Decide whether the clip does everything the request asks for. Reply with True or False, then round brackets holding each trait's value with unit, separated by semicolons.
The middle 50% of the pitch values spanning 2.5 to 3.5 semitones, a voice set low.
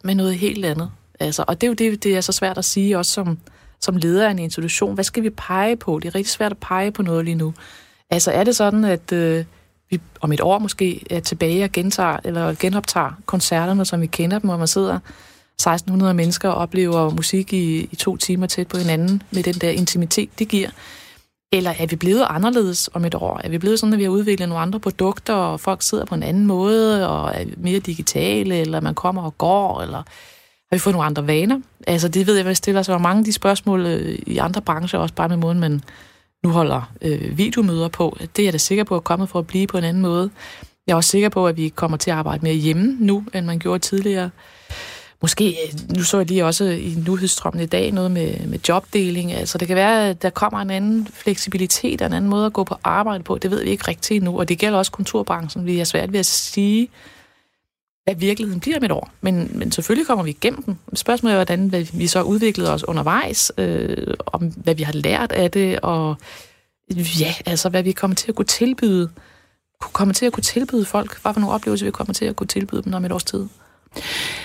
False (3.1 semitones; 185 Hz)